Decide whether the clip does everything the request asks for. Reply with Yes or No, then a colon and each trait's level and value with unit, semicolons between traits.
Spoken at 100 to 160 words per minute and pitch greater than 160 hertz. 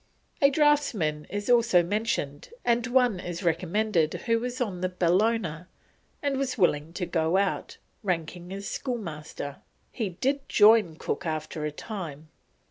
Yes: average, 140 wpm; high, 190 Hz